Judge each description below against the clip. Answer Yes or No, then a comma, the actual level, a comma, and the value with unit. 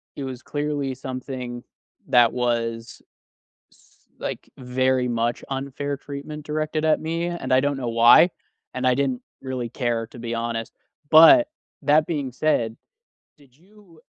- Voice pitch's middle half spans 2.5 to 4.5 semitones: Yes, average, 3.7 semitones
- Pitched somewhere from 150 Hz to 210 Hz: No, low, 130 Hz